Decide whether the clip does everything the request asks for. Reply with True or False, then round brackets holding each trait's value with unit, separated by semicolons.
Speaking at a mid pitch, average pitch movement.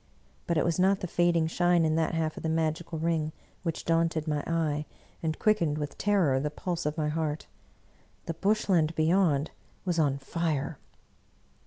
False (160 Hz; 1.9 semitones)